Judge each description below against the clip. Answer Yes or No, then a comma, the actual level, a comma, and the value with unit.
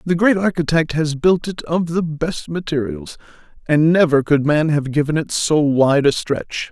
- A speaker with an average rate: Yes, average, 190 wpm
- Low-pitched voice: No, medium, 155 Hz